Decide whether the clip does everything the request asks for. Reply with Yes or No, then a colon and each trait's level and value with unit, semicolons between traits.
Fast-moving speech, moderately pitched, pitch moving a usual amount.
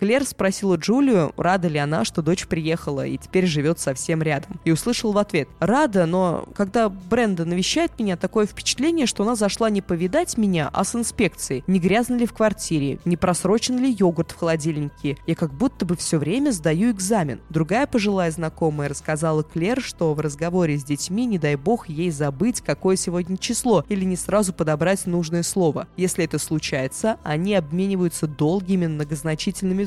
Yes: fast, 170 wpm; medium, 180 Hz; average, 4.5 semitones